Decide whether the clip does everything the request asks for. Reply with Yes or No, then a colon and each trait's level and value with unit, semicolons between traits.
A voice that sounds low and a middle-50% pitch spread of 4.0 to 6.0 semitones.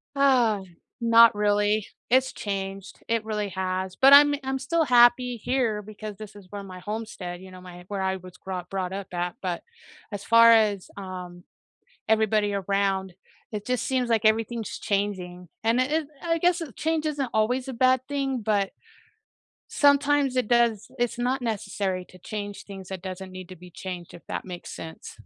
No: high, 210 Hz; average, 4.6 semitones